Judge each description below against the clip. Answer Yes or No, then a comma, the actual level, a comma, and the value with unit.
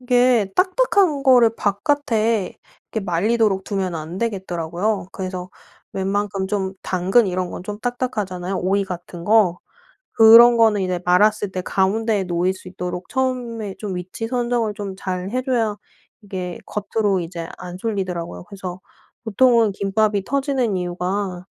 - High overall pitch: Yes, high, 200 Hz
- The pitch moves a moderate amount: Yes, average, 3.8 semitones